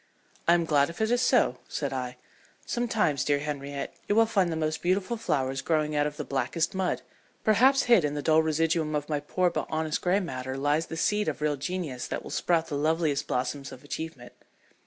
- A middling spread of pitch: Yes, average, 3.9 semitones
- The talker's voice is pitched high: No, medium, 155 Hz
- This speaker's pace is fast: Yes, fast, 210 wpm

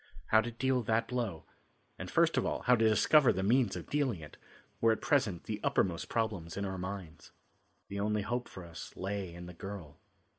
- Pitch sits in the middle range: No, low, 100 Hz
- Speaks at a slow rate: No, average, 200 wpm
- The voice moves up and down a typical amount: Yes, average, 4.1 semitones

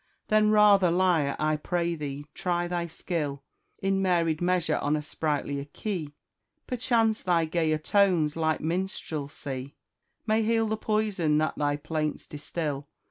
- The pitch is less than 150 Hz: No, medium, 165 Hz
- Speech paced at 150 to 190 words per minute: No, slow, 135 wpm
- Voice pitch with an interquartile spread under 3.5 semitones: No, average, 4.3 semitones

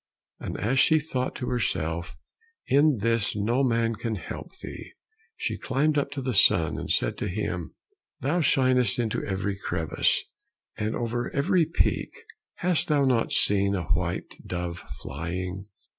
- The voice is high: No, low, 115 Hz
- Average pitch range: No, wide, 5.9 semitones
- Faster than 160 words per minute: No, average, 150 wpm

